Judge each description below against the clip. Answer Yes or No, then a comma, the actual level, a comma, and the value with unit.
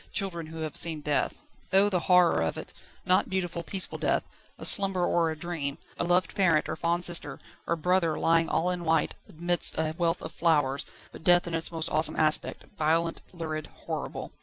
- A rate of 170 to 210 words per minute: Yes, average, 190 wpm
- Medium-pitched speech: Yes, medium, 165 Hz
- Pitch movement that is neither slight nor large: No, narrow, 2.0 semitones